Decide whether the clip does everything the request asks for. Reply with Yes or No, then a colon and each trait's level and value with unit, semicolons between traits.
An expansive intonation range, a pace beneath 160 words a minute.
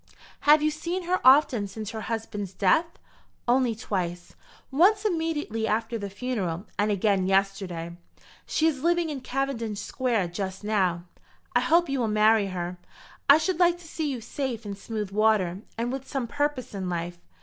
No: wide, 6.7 semitones; average, 170 wpm